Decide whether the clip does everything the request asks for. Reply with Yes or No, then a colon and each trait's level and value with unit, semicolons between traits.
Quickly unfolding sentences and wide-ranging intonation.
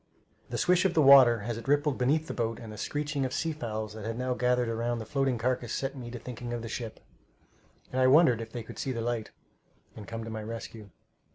No: fast, 245 wpm; average, 2.9 semitones